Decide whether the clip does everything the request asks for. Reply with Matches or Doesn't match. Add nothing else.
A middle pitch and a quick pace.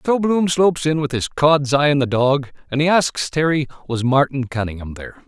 Matches